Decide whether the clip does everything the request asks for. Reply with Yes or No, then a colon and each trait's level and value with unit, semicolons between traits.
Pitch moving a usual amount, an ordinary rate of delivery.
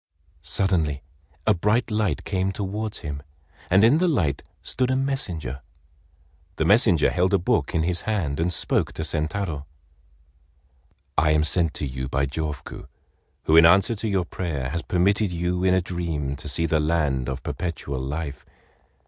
Yes: average, 4.7 semitones; average, 165 wpm